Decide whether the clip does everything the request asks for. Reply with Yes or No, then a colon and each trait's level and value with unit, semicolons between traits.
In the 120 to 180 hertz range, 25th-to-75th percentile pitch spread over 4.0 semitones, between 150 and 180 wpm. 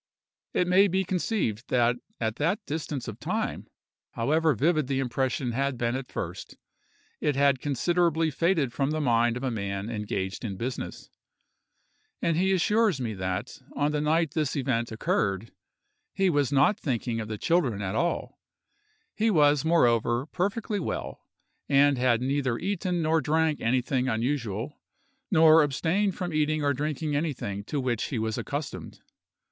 Yes: medium, 140 Hz; wide, 5.4 semitones; average, 155 wpm